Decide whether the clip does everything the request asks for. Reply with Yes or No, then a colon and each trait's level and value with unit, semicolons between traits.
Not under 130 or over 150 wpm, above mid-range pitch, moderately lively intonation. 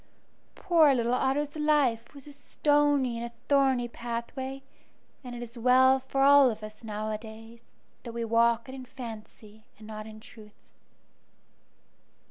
Yes: average, 145 wpm; high, 240 Hz; average, 3.2 semitones